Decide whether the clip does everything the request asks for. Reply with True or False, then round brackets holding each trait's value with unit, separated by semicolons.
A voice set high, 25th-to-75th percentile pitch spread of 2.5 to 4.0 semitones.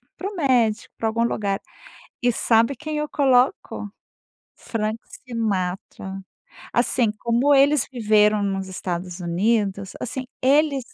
False (230 Hz; 4.6 semitones)